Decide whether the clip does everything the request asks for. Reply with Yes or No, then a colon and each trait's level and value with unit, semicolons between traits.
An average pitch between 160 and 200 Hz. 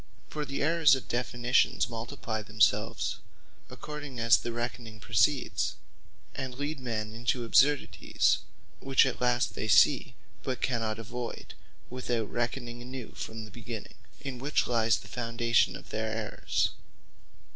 No: low, 120 Hz